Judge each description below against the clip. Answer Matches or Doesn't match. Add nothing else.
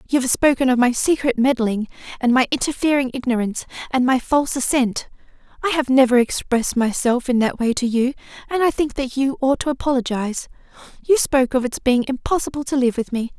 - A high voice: Matches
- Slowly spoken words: Doesn't match